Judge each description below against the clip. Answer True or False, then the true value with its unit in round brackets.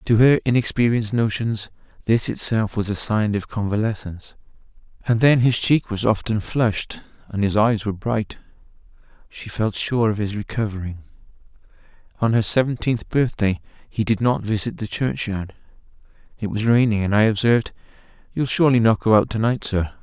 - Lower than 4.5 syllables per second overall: False (5.1 syllables/s)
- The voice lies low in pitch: True (110 Hz)